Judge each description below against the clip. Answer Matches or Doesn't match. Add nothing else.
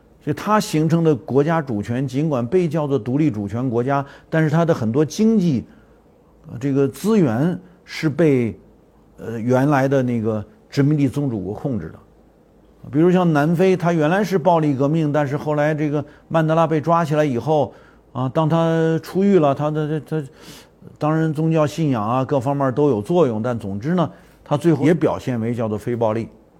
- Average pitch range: Matches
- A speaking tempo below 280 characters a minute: Matches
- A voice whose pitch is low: Doesn't match